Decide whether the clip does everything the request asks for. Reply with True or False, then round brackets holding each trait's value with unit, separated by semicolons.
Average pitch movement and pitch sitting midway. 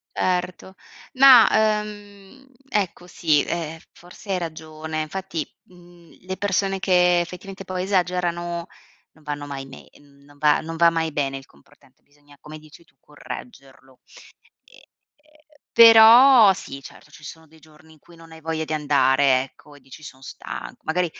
True (3.9 semitones; 165 Hz)